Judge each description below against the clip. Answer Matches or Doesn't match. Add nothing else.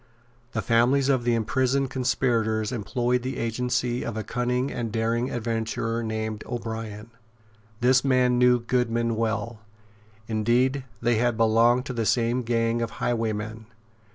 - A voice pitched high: Doesn't match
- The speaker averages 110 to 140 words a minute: Matches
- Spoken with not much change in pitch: Matches